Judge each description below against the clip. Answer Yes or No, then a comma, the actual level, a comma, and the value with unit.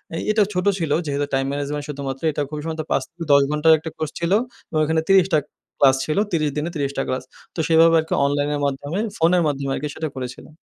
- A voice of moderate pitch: Yes, medium, 150 Hz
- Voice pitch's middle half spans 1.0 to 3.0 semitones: Yes, narrow, 2.5 semitones